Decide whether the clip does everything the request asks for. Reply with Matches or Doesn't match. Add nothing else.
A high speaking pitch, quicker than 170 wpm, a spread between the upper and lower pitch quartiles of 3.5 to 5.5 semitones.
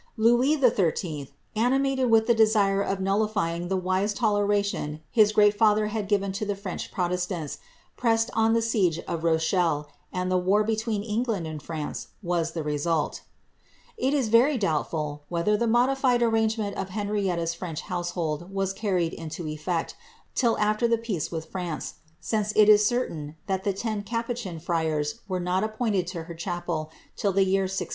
Doesn't match